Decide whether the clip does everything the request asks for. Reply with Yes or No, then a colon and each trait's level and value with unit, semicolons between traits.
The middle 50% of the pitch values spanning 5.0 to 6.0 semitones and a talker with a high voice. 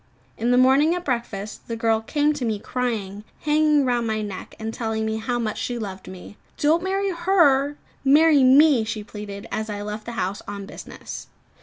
Yes: wide, 5.4 semitones; high, 235 Hz